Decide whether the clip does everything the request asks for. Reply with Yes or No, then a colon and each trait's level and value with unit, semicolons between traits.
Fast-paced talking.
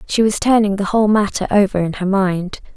Yes: fast, 215 wpm